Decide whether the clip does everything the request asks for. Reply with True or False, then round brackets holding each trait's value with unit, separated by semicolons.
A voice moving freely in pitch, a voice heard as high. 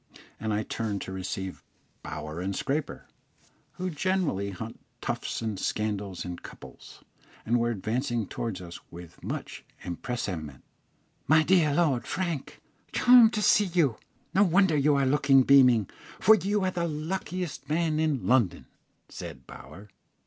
False (9.0 semitones; 130 Hz)